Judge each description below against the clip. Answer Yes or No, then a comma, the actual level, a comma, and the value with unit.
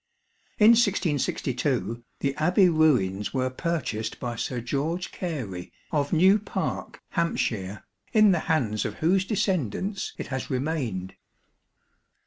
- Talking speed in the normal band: No, slow, 115 wpm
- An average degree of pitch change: No, wide, 7.1 semitones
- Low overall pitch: No, medium, 150 Hz